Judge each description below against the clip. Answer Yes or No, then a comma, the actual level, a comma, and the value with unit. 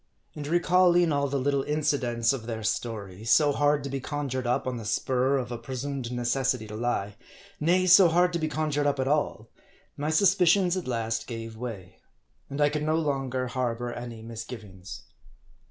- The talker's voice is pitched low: Yes, low, 130 Hz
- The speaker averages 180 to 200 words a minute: Yes, average, 185 wpm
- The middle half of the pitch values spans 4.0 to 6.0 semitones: Yes, average, 4.3 semitones